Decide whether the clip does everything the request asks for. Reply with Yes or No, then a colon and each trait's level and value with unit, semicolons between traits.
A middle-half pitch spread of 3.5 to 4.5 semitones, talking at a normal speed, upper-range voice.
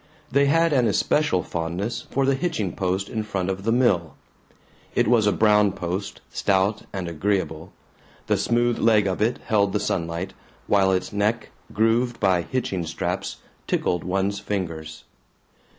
No: average, 3.8 semitones; average, 150 wpm; low, 100 Hz